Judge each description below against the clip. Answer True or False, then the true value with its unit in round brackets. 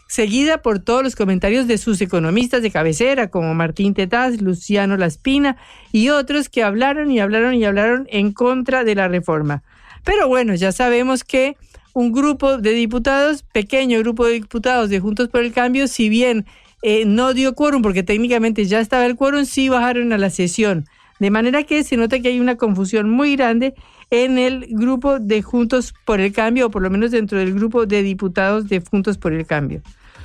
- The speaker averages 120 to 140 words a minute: False (190 wpm)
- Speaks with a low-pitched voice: False (230 Hz)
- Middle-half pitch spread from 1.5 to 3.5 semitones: False (3.9 semitones)